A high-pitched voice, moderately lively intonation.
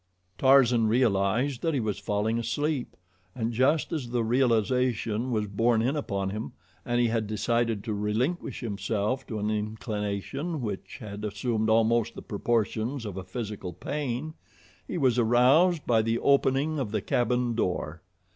No: low, 115 Hz; average, 3.3 semitones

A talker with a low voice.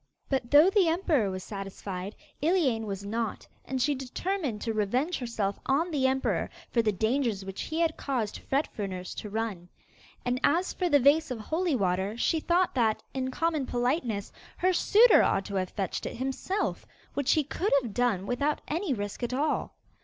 No: very high, 255 Hz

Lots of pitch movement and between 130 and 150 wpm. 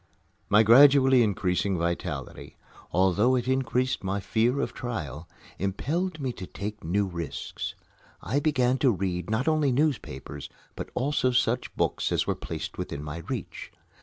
Yes: wide, 6.0 semitones; average, 145 wpm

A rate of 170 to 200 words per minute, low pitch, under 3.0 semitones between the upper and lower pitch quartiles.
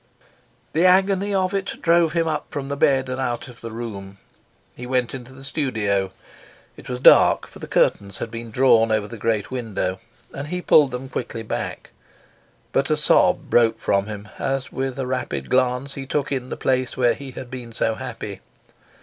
No: average, 190 wpm; low, 125 Hz; average, 3.4 semitones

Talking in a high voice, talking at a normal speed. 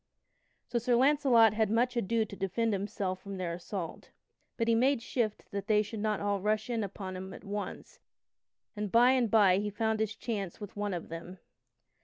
Yes: high, 210 Hz; average, 195 wpm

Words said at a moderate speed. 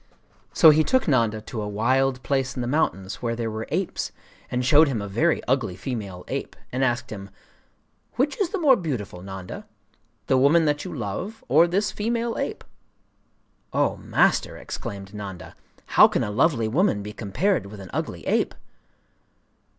Yes: average, 170 wpm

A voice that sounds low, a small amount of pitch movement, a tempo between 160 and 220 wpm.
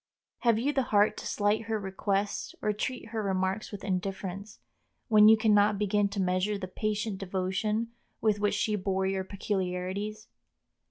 No: high, 205 Hz; narrow, 1.9 semitones; average, 165 wpm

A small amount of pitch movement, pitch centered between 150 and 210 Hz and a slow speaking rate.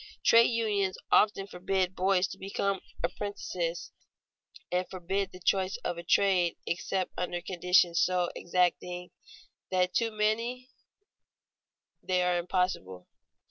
Yes: narrow, 1.8 semitones; medium, 185 Hz; slow, 115 wpm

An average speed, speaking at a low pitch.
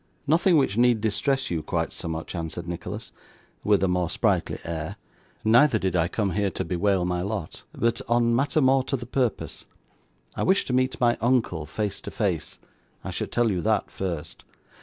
Yes: average, 185 wpm; low, 105 Hz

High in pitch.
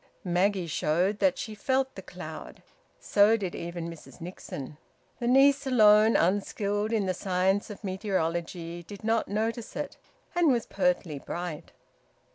Yes: high, 200 Hz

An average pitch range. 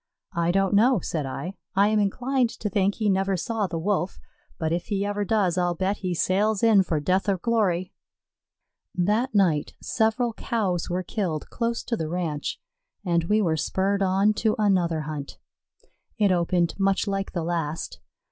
Yes: average, 3.3 semitones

